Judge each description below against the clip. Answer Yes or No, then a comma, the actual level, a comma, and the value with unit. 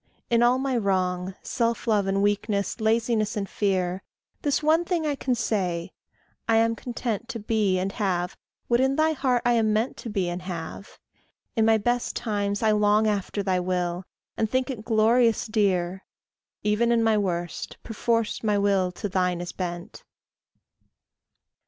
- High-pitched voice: Yes, high, 210 Hz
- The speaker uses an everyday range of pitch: Yes, average, 3.6 semitones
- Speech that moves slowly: No, average, 165 wpm